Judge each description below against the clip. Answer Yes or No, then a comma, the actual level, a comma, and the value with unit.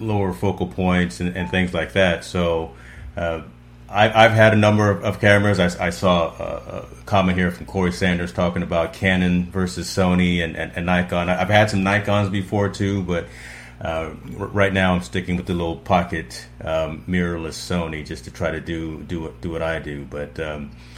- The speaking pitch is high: No, very low, 90 Hz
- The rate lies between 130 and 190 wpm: No, average, 200 wpm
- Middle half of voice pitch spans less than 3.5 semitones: Yes, average, 2.9 semitones